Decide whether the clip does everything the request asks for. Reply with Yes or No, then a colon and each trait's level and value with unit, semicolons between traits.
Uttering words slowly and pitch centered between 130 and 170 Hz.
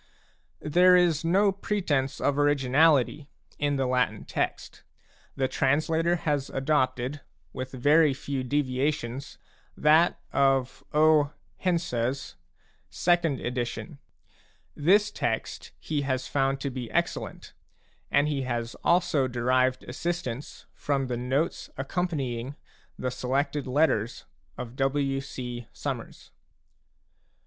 Yes: slow, 105 wpm; medium, 140 Hz